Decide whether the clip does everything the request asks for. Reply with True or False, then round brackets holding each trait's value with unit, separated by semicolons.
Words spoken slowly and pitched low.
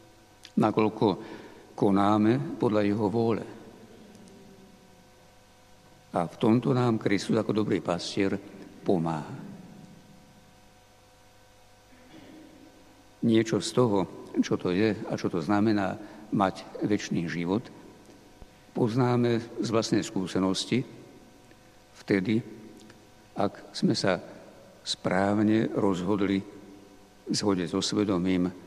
True (85 wpm; 105 Hz)